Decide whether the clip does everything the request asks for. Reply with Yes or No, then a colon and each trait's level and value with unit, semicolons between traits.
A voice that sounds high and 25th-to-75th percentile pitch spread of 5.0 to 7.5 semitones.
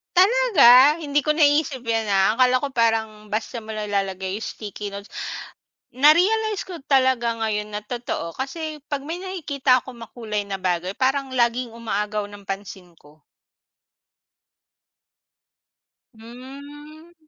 Yes: high, 240 Hz; wide, 5.5 semitones